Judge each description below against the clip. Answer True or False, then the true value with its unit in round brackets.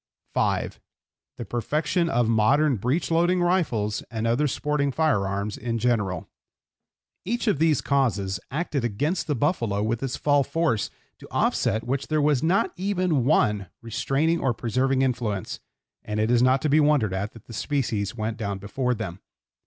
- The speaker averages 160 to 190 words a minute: True (165 wpm)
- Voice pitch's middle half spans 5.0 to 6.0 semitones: True (5.6 semitones)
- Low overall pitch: True (125 Hz)